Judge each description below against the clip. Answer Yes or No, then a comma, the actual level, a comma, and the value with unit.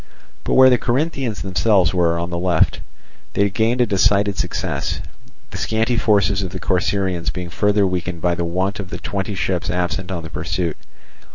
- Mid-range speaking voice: No, very low, 95 Hz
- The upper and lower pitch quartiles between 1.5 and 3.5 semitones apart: Yes, average, 2.8 semitones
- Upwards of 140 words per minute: Yes, average, 180 wpm